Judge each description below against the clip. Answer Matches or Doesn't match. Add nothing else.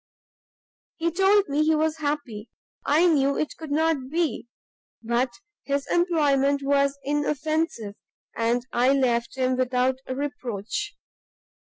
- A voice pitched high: Matches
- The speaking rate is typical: Doesn't match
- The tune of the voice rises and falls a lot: Doesn't match